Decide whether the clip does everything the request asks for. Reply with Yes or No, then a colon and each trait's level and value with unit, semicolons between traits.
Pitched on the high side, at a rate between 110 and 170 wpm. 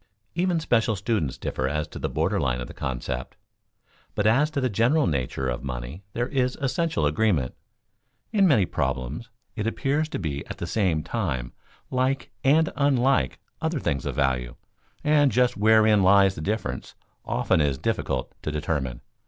No: low, 105 Hz; average, 165 wpm